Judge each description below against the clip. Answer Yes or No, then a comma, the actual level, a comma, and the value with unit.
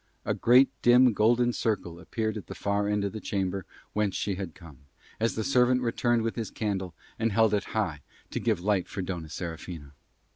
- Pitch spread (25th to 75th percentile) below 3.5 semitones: No, average, 3.8 semitones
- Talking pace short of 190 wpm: No, average, 195 wpm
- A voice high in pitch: No, low, 105 Hz